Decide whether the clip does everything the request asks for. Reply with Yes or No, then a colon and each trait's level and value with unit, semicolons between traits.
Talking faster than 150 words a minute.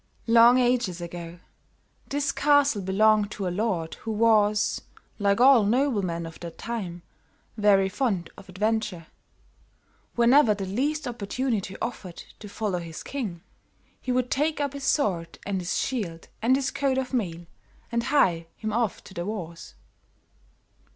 No: average, 145 wpm